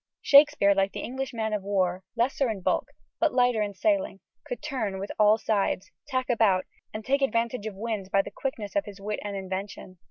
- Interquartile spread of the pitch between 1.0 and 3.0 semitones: No, average, 4.4 semitones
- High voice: Yes, high, 215 Hz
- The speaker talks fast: Yes, fast, 210 wpm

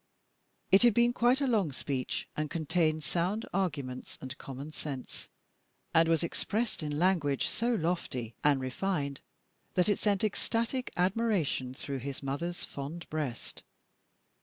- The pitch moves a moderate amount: No, wide, 6.3 semitones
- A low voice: No, medium, 165 Hz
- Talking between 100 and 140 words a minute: Yes, slow, 135 wpm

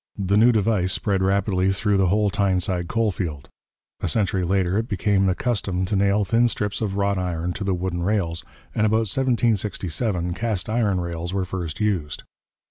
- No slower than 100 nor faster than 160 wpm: No, average, 180 wpm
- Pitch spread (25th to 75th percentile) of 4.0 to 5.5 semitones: No, average, 2.8 semitones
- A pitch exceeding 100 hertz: No, very low, 95 Hz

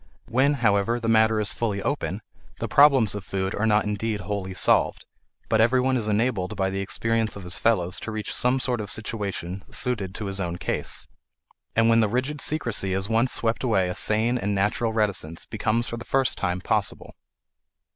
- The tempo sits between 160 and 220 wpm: Yes, average, 190 wpm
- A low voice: Yes, low, 110 Hz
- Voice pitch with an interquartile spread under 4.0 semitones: Yes, average, 3.1 semitones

